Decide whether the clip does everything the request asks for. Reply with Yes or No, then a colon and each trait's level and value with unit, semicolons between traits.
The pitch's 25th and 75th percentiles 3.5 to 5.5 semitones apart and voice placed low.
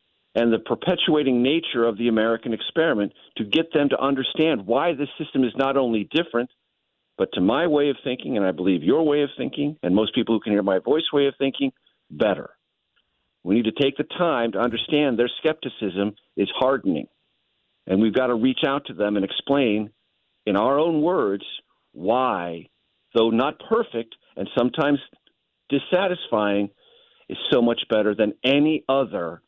Yes: average, 4.7 semitones; low, 125 Hz